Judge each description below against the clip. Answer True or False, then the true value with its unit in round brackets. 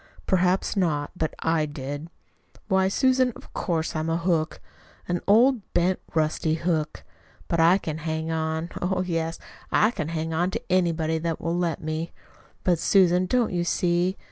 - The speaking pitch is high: False (170 Hz)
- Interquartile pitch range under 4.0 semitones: True (2.5 semitones)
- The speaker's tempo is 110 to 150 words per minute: False (165 wpm)